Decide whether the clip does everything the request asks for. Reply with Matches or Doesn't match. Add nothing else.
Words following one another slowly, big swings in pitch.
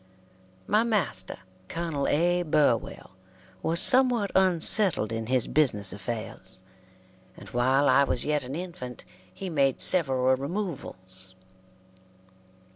Matches